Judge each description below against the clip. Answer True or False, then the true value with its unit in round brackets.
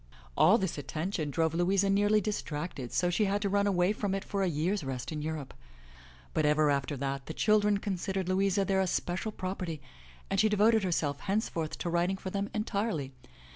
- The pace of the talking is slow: False (185 wpm)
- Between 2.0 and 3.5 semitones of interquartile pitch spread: False (4.3 semitones)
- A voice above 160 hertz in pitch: True (185 Hz)